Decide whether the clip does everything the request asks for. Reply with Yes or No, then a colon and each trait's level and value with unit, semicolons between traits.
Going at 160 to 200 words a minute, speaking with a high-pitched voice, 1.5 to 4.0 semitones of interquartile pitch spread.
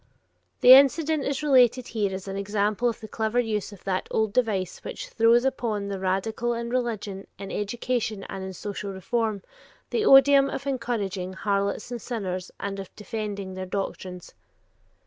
Yes: average, 165 wpm; high, 215 Hz; average, 3.7 semitones